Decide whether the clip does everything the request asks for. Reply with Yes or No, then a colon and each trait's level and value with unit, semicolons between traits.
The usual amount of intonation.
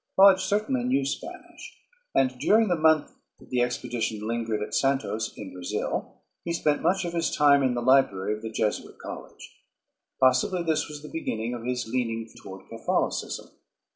No: wide, 6.7 semitones